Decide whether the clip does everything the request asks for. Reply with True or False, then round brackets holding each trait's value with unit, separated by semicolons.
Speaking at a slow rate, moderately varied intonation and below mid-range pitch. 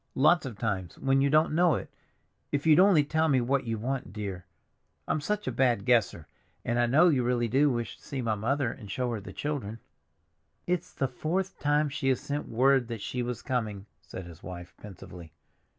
False (205 wpm; 5.0 semitones; 125 Hz)